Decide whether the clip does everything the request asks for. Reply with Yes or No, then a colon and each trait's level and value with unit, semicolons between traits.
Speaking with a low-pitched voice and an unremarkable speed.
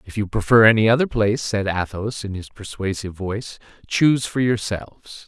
Yes: low, 110 Hz; average, 170 wpm